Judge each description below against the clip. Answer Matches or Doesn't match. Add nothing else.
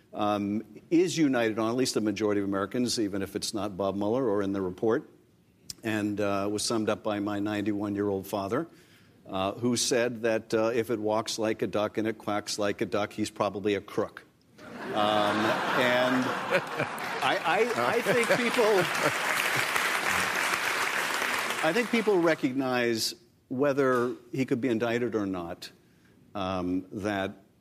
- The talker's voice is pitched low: Matches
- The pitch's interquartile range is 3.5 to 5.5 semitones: Doesn't match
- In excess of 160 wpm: Doesn't match